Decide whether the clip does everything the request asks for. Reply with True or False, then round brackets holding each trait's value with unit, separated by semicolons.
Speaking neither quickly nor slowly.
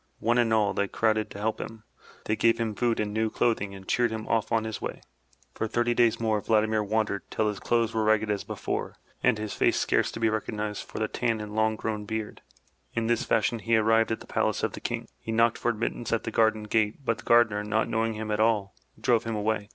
False (235 wpm)